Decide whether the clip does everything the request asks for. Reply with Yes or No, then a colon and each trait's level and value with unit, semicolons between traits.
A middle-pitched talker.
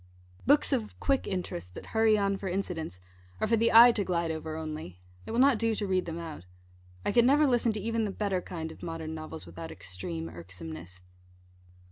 Yes: medium, 180 Hz